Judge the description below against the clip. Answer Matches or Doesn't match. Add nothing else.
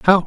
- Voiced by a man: Matches